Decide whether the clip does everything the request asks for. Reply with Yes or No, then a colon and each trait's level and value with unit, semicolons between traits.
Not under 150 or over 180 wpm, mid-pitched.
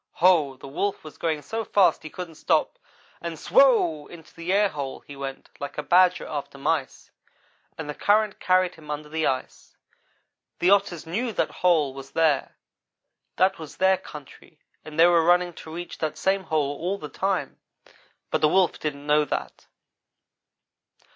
Yes: average, 165 wpm; medium, 160 Hz